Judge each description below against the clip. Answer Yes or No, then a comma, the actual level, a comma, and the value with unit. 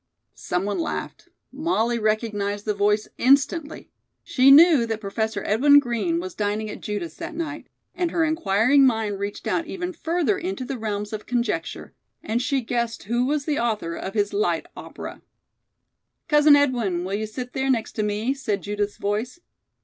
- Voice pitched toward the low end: No, high, 230 Hz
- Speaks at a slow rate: No, average, 170 wpm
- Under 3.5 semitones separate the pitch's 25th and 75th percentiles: No, wide, 5.5 semitones